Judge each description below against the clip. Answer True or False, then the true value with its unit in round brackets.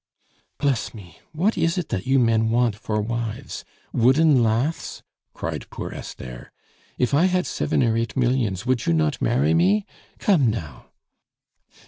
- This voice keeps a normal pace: True (150 wpm)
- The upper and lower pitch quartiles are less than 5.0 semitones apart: True (4.6 semitones)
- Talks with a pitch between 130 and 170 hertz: False (115 Hz)